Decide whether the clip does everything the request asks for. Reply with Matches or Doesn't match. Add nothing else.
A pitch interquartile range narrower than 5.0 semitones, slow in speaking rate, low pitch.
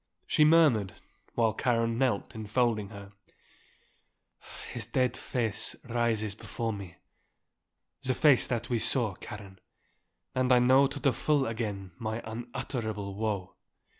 Matches